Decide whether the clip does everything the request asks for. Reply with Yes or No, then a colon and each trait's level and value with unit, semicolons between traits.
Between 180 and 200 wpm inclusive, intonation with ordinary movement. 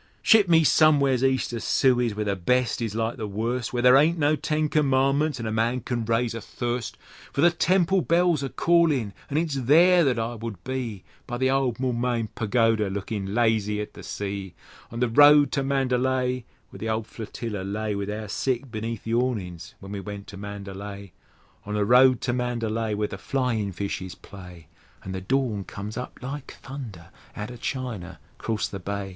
Yes: average, 190 wpm; average, 4.2 semitones